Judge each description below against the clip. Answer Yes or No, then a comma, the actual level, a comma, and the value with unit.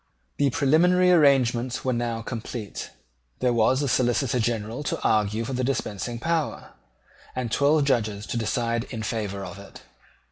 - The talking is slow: No, average, 150 wpm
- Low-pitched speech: Yes, low, 120 Hz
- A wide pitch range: No, average, 3.5 semitones